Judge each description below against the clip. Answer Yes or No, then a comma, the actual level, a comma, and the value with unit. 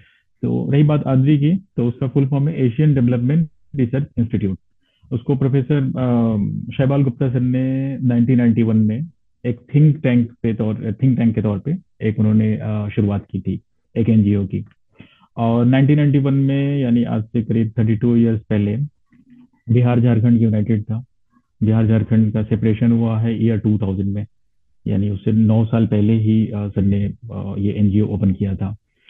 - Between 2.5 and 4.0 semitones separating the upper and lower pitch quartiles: Yes, average, 3.6 semitones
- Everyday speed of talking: Yes, average, 155 wpm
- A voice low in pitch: Yes, low, 115 Hz